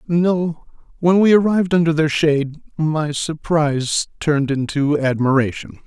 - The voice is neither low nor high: Yes, medium, 155 Hz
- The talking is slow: Yes, slow, 125 wpm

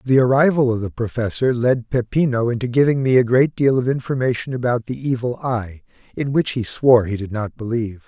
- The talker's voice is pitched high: No, low, 120 Hz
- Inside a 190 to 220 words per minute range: Yes, average, 200 wpm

